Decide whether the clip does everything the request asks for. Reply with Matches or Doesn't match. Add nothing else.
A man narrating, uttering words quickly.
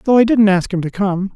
Matches